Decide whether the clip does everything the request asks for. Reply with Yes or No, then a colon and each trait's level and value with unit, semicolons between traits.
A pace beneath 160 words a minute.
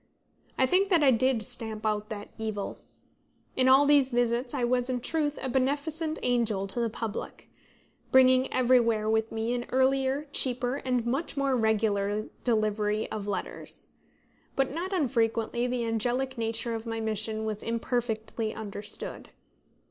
Yes: average, 150 wpm